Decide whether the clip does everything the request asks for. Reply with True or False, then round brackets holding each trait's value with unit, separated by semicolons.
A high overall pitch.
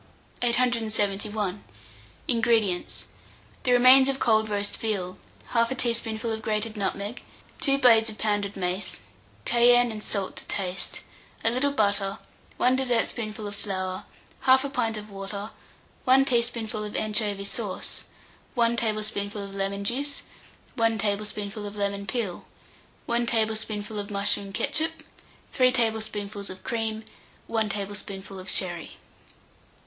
True (215 Hz)